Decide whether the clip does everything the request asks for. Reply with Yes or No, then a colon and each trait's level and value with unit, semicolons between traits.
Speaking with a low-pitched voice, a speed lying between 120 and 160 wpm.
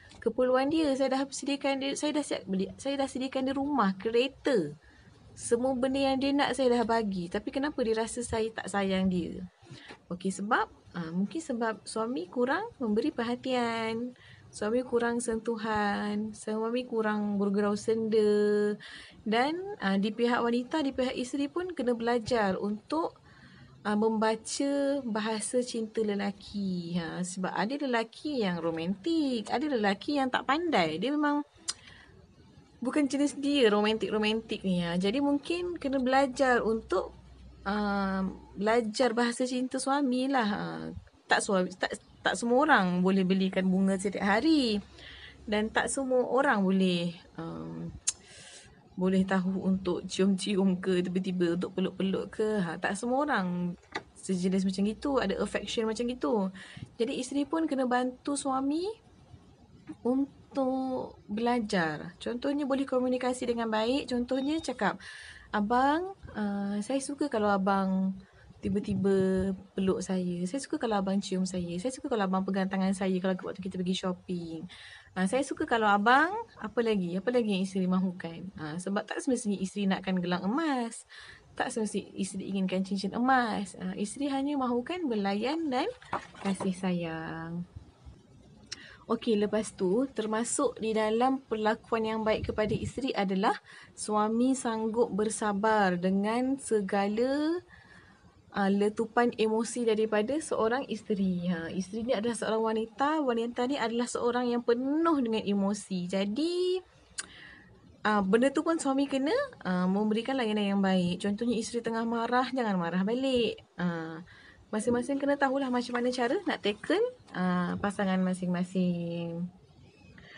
No: high, 220 Hz; average, 135 wpm